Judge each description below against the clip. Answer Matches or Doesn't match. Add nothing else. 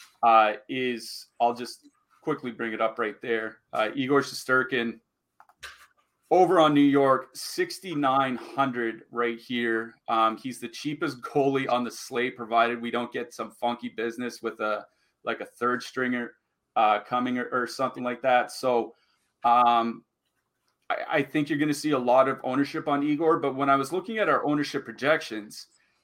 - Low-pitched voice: Matches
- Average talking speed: Matches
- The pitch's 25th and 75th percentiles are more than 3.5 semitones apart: Doesn't match